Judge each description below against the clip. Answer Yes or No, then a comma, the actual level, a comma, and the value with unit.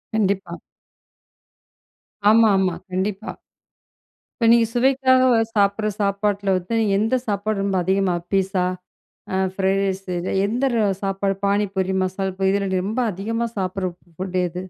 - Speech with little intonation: Yes, narrow, 2.2 semitones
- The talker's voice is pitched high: Yes, high, 195 Hz